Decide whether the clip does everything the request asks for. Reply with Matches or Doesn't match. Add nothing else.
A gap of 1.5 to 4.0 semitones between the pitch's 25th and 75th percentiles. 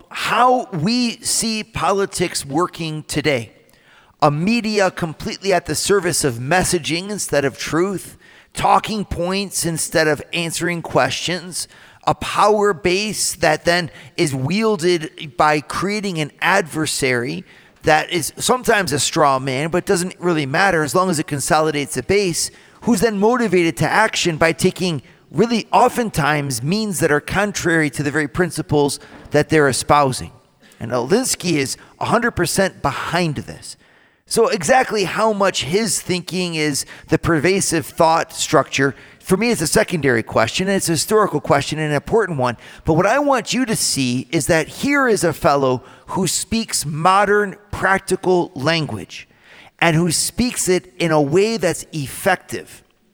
Doesn't match